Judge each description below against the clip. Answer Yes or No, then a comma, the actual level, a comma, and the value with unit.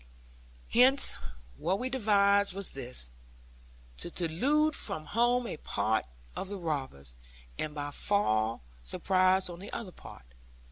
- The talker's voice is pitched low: No, medium, 185 Hz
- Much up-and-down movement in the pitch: Yes, wide, 7.6 semitones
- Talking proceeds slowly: Yes, slow, 130 wpm